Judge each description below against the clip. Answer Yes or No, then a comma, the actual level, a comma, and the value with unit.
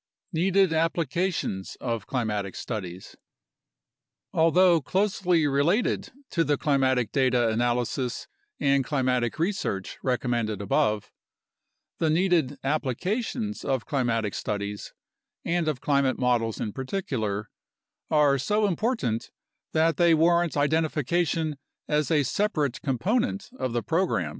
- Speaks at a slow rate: Yes, slow, 110 wpm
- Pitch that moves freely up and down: Yes, wide, 6.0 semitones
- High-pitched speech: No, medium, 140 Hz